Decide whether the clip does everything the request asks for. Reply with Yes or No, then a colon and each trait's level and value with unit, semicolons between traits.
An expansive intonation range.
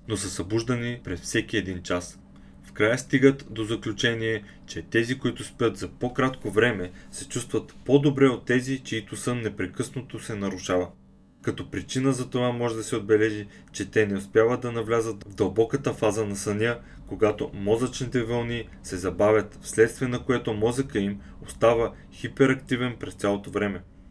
No: average, 3.6 semitones